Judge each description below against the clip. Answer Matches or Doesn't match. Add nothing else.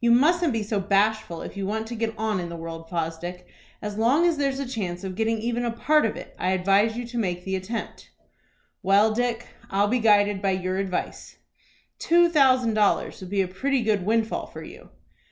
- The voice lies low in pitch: Doesn't match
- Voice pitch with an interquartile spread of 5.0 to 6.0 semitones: Doesn't match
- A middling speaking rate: Doesn't match